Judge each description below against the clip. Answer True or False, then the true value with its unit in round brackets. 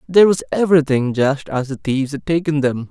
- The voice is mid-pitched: True (145 Hz)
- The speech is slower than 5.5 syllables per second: False (6.0 syllables/s)